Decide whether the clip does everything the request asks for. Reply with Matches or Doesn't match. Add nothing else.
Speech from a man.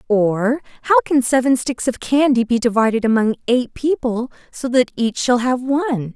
Doesn't match